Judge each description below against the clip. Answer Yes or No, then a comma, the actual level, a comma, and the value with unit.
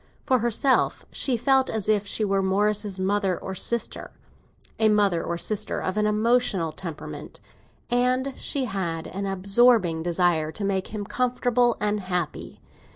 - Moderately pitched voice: No, high, 205 Hz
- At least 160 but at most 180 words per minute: No, average, 140 wpm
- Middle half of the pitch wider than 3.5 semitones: Yes, average, 4.1 semitones